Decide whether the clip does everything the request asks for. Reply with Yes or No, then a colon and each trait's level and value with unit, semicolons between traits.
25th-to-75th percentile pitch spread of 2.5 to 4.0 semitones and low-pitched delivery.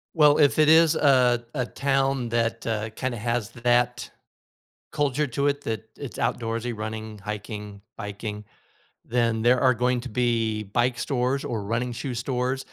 Yes: average, 2.9 semitones; low, 120 Hz